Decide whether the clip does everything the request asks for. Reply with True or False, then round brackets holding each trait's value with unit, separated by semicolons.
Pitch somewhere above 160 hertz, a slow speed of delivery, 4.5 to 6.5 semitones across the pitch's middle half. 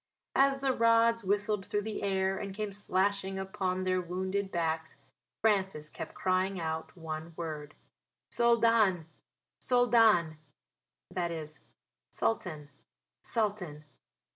False (190 Hz; 110 wpm; 4.1 semitones)